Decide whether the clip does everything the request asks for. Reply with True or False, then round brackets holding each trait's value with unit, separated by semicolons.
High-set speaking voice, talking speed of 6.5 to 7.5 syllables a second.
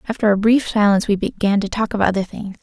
True (205 Hz; 6.6 syllables/s)